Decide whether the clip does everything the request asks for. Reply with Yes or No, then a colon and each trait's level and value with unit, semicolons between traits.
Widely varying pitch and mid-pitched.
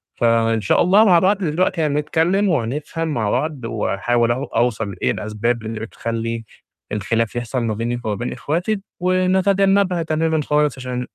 No: wide, 6.8 semitones; low, 130 Hz